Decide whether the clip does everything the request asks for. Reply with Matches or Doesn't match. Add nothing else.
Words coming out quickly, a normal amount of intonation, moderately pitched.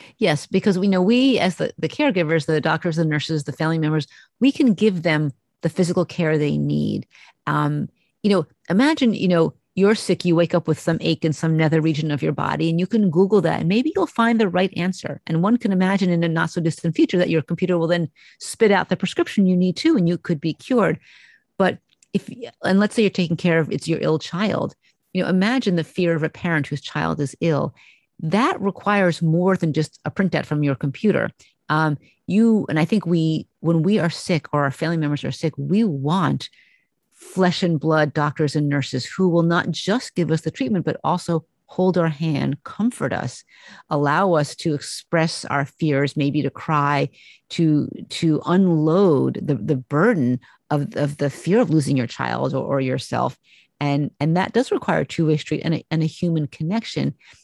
Matches